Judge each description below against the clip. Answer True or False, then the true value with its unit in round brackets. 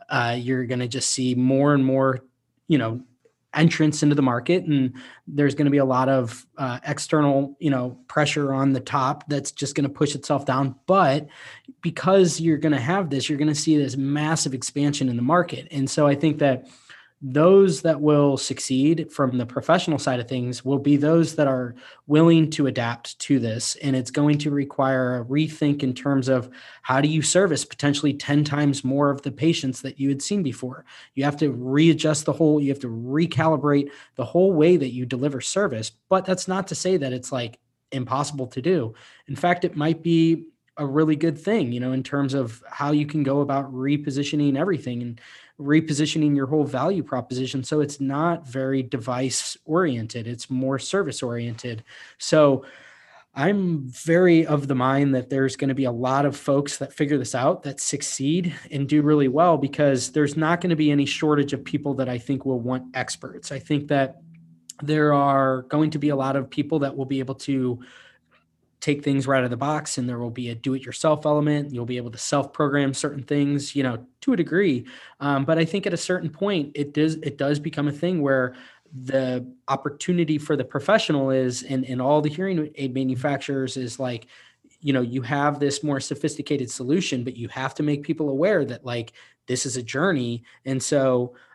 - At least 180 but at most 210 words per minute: True (205 wpm)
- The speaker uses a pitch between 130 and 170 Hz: True (140 Hz)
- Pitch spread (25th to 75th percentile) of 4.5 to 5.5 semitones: False (2.5 semitones)